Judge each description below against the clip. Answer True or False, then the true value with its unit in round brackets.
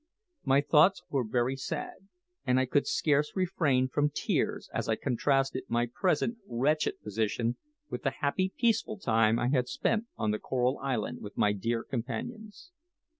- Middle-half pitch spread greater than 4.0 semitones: True (4.8 semitones)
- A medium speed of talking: True (160 wpm)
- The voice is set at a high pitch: False (135 Hz)